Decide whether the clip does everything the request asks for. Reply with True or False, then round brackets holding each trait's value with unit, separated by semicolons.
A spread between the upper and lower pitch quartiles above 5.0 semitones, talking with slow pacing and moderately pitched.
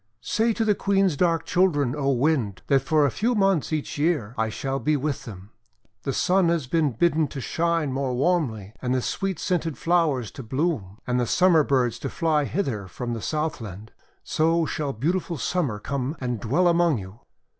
False (5.5 semitones; 190 wpm; 145 Hz)